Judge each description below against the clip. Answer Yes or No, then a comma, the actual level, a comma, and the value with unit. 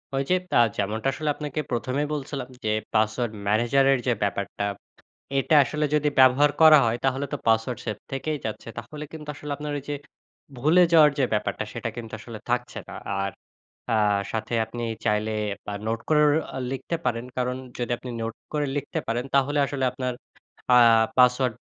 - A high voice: No, low, 125 Hz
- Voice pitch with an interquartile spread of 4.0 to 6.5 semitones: Yes, average, 4.3 semitones